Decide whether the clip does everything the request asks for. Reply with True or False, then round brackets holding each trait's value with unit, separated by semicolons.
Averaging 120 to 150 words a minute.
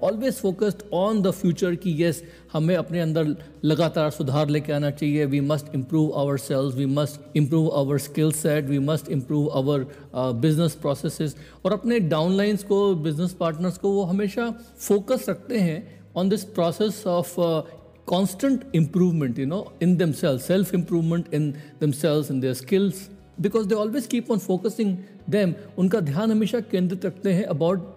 False (165 wpm)